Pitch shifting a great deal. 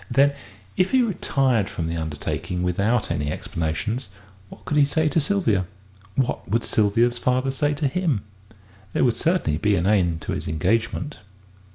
Yes: wide, 7.9 semitones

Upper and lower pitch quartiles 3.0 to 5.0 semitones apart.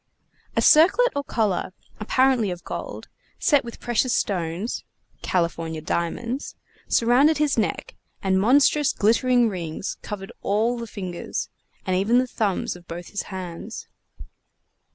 No: wide, 5.4 semitones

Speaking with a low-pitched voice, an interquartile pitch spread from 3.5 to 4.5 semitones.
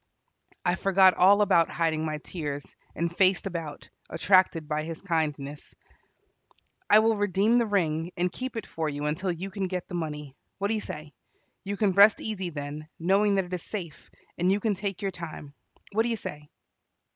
No: medium, 180 Hz; average, 4.2 semitones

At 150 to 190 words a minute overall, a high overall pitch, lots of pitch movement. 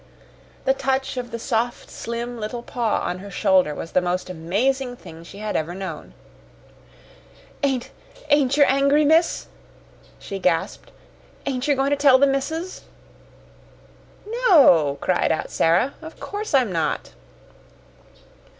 No: slow, 135 wpm; high, 245 Hz; wide, 7.2 semitones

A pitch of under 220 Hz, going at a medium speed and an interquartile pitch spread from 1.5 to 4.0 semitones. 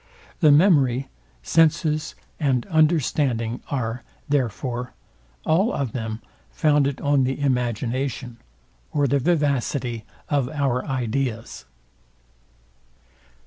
No: low, 135 Hz; slow, 90 wpm; average, 3.3 semitones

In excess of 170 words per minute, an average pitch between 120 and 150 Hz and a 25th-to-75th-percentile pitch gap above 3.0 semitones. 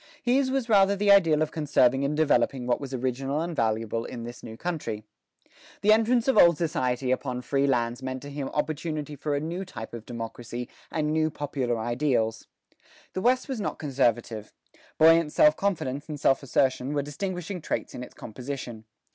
Yes: average, 180 wpm; medium, 140 Hz; average, 4.9 semitones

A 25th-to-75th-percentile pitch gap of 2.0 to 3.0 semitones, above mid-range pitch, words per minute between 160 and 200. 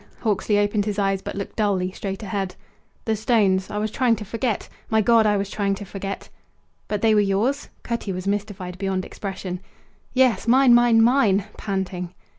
Yes: narrow, 2.5 semitones; high, 205 Hz; average, 180 wpm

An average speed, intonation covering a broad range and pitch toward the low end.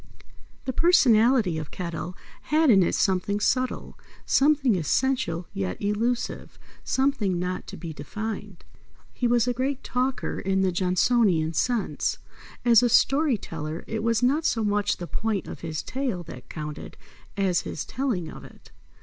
No: average, 150 wpm; wide, 6.0 semitones; high, 210 Hz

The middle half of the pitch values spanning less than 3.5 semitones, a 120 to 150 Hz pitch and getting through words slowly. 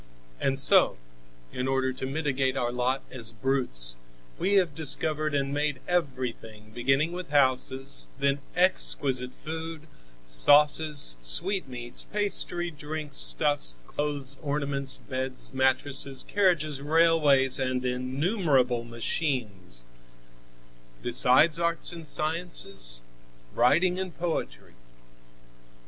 No: average, 3.8 semitones; medium, 140 Hz; slow, 100 wpm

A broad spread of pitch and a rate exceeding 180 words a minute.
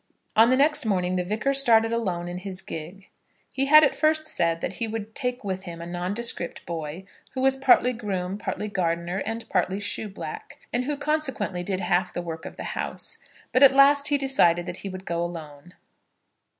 Yes: wide, 6.4 semitones; average, 195 wpm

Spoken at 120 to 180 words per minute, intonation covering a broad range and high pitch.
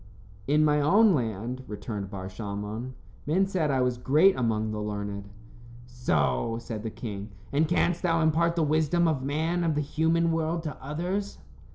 No: average, 175 wpm; wide, 7.1 semitones; medium, 145 Hz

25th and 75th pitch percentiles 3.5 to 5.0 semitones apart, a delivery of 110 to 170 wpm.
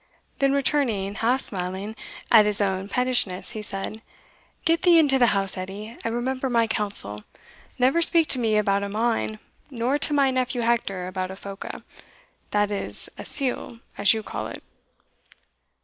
Yes: average, 4.5 semitones; average, 165 wpm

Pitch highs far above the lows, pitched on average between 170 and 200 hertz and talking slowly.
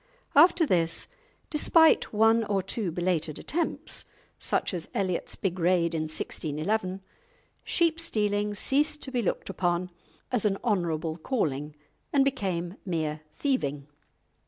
Yes: wide, 6.3 semitones; high, 190 Hz; slow, 125 wpm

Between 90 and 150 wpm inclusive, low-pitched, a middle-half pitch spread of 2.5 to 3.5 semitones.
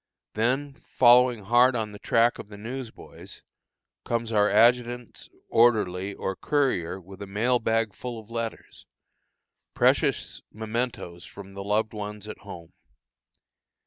Yes: slow, 135 wpm; low, 110 Hz; average, 2.9 semitones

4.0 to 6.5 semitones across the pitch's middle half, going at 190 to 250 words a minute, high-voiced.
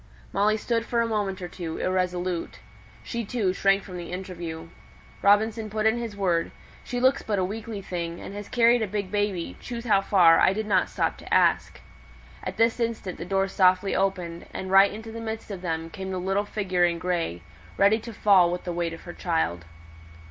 No: average, 3.3 semitones; fast, 205 wpm; high, 195 Hz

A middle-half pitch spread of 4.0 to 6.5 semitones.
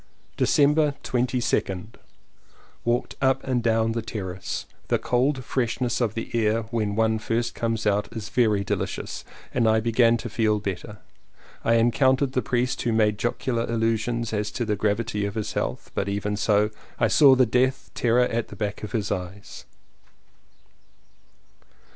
No: narrow, 2.5 semitones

